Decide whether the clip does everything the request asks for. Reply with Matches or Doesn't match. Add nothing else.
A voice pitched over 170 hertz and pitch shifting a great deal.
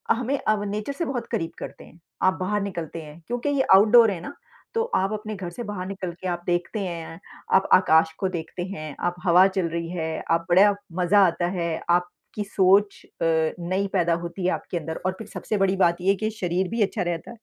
Doesn't match